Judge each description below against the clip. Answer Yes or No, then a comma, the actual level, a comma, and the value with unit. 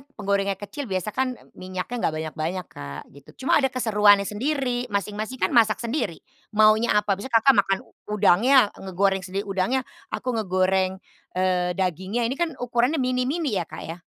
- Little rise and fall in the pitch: No, average, 4.8 semitones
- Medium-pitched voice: No, high, 205 Hz